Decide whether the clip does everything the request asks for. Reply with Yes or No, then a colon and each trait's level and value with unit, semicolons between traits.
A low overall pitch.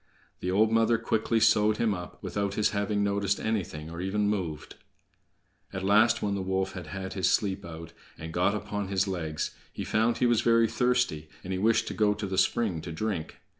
Yes: low, 100 Hz